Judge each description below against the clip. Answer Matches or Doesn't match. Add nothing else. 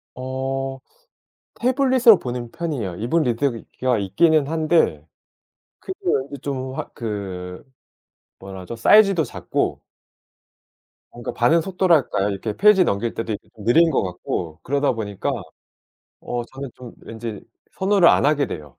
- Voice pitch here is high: Doesn't match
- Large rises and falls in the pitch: Matches